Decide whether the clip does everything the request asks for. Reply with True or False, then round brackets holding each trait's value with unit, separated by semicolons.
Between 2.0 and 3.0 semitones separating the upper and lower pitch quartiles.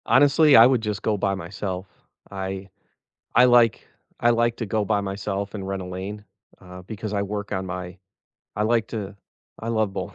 True (2.7 semitones)